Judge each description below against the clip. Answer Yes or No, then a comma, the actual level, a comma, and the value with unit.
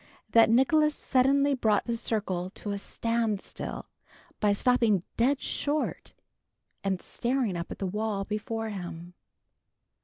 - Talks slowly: Yes, slow, 130 wpm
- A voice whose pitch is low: No, high, 220 Hz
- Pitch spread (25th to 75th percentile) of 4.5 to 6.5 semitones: No, average, 4.0 semitones